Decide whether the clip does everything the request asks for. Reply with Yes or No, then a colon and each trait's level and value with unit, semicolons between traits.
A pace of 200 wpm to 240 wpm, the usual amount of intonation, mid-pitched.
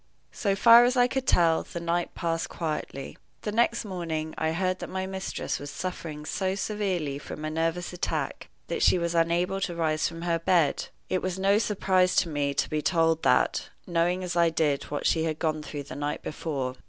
Yes: fast, 205 wpm; average, 3.2 semitones; medium, 170 Hz